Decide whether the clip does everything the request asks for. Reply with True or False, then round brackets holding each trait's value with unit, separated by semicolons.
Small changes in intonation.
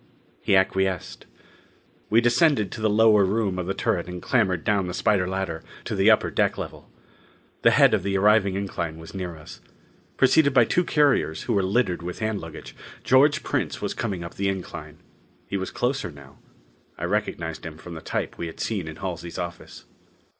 False (4.1 semitones)